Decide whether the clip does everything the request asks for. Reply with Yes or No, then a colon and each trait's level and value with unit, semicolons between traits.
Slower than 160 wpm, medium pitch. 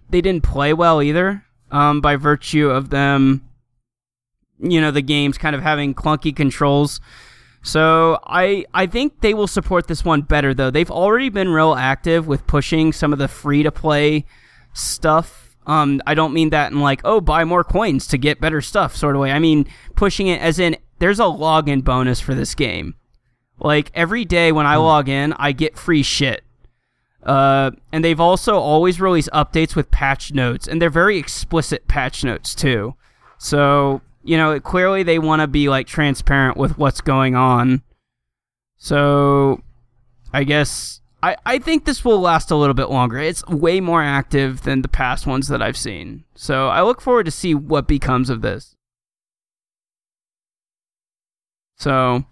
No: average, 170 wpm; medium, 150 Hz